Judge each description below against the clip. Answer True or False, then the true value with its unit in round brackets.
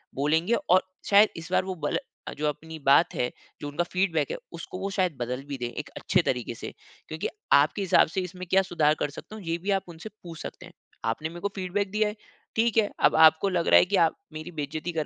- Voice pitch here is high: False (170 Hz)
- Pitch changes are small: False (3.8 semitones)